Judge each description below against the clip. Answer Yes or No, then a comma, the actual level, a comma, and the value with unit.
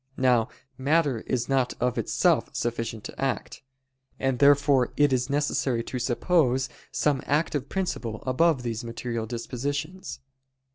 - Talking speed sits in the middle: No, slow, 130 wpm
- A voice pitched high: No, low, 130 Hz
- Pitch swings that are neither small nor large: Yes, average, 3.0 semitones